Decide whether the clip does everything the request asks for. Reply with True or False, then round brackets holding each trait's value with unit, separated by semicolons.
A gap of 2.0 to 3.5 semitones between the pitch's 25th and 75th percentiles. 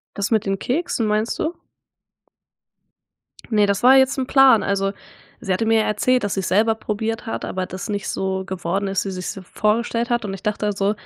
True (2.8 semitones)